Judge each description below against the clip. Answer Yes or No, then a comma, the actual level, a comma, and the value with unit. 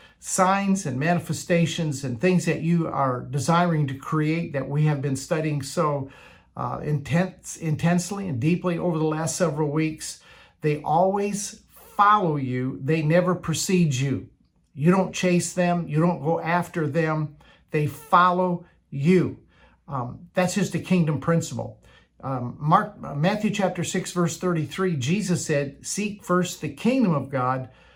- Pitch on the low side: No, medium, 165 Hz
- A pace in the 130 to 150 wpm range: Yes, average, 145 wpm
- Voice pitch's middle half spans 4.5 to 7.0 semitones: No, average, 3.5 semitones